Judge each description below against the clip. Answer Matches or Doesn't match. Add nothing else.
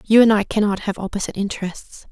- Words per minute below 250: Matches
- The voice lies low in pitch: Doesn't match